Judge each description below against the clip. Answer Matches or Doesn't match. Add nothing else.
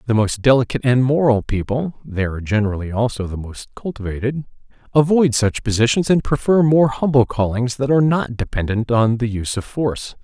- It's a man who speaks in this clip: Matches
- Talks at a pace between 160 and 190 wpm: Matches